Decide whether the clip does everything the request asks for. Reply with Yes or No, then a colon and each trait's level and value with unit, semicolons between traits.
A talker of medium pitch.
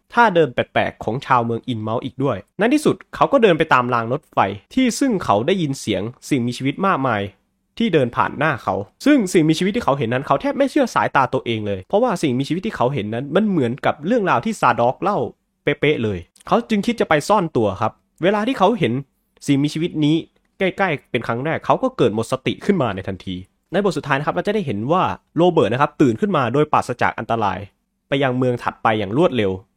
Yes: medium, 145 Hz